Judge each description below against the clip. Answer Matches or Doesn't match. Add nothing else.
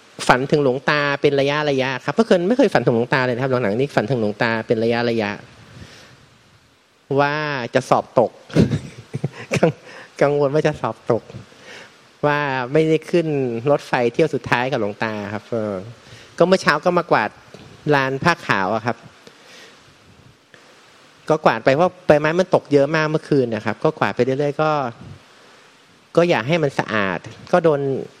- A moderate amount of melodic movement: Matches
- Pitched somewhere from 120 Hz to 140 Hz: Matches